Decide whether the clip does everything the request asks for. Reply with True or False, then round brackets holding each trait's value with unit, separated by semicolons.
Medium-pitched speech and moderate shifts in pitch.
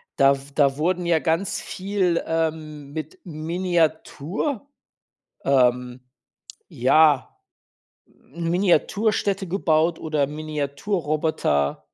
True (160 Hz; 3.7 semitones)